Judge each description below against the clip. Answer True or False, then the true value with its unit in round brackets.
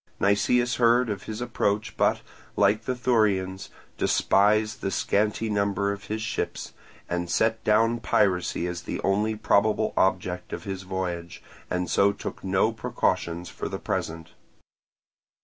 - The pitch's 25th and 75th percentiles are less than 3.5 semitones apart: True (2.8 semitones)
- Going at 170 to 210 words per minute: False (140 wpm)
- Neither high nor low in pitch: False (100 Hz)